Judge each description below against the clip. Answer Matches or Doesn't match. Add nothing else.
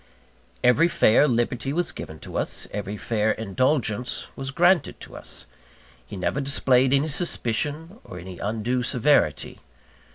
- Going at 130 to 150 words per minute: Matches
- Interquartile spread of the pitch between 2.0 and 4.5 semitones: Doesn't match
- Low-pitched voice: Matches